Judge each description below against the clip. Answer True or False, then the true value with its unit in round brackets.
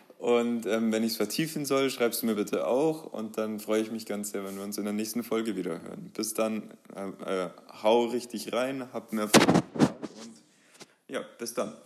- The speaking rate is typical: False (210 wpm)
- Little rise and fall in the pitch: True (2.0 semitones)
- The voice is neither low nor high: False (110 Hz)